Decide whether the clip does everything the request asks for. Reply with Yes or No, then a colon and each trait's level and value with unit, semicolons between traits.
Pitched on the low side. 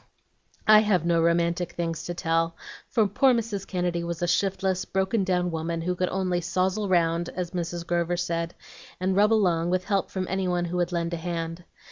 No: medium, 175 Hz